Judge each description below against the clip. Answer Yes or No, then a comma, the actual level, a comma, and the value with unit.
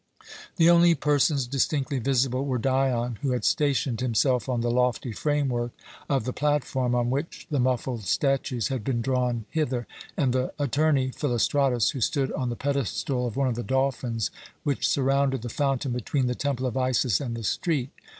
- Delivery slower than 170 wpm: No, average, 175 wpm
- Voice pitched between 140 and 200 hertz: No, low, 130 Hz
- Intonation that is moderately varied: No, narrow, 2.3 semitones